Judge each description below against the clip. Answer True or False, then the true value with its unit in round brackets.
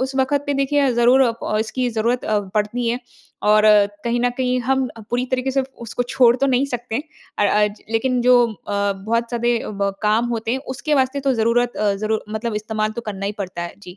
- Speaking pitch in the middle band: False (235 Hz)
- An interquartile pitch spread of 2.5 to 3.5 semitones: True (3.0 semitones)